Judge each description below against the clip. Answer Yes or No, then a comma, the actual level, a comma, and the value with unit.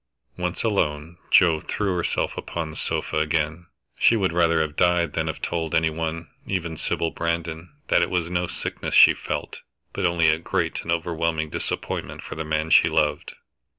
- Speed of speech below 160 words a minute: No, average, 180 wpm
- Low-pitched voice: Yes, very low, 85 Hz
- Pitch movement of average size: No, narrow, 1.6 semitones